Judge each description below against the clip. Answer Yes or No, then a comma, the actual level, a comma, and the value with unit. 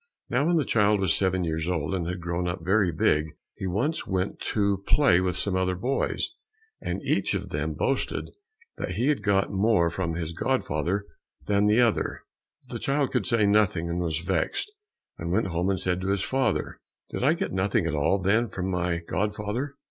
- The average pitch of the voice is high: No, very low, 95 Hz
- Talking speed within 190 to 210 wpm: Yes, average, 195 wpm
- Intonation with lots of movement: No, average, 3.4 semitones